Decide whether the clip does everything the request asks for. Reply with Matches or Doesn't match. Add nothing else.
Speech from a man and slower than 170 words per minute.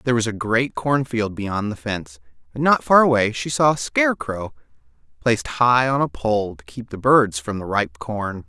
Doesn't match